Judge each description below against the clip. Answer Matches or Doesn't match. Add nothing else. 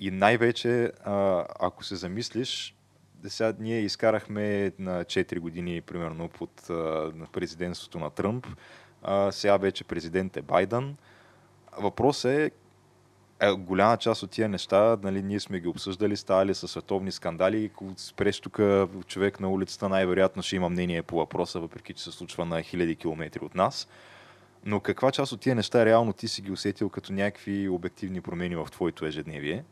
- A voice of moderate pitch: Doesn't match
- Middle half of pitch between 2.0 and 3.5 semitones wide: Matches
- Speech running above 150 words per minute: Matches